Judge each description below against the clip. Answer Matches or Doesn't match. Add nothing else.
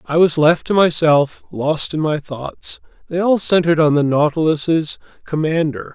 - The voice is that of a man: Matches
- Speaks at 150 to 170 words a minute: Matches